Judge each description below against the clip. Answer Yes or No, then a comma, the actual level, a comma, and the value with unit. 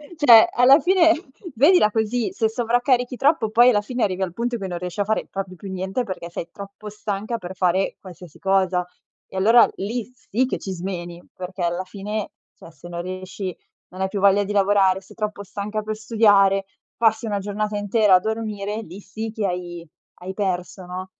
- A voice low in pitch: No, high, 200 Hz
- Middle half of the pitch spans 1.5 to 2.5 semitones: No, average, 2.9 semitones